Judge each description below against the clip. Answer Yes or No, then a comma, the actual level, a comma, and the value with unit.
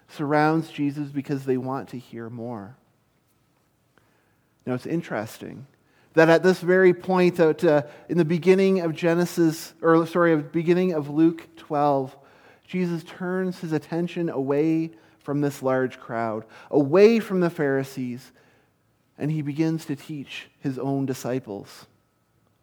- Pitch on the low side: No, medium, 145 Hz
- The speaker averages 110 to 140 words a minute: Yes, slow, 135 wpm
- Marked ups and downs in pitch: No, average, 4.4 semitones